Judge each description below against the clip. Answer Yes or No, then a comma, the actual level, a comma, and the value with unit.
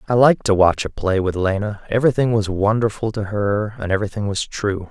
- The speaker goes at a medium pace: No, fast, 210 wpm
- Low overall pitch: Yes, low, 105 Hz